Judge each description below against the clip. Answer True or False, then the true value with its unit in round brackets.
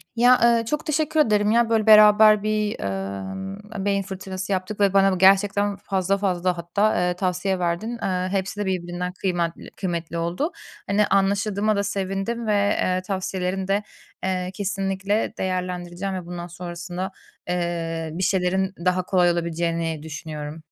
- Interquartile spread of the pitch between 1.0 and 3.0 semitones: True (2.5 semitones)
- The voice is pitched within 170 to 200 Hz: True (190 Hz)